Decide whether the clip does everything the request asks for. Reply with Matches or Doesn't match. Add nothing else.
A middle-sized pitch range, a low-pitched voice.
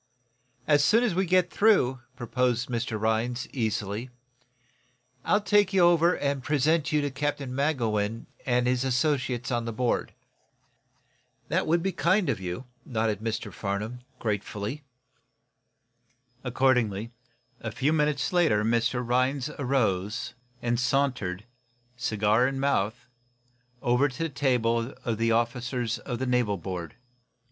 Matches